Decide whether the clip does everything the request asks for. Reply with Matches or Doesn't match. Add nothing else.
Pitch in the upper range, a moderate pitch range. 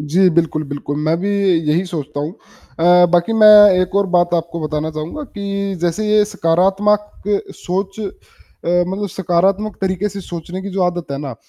Doesn't match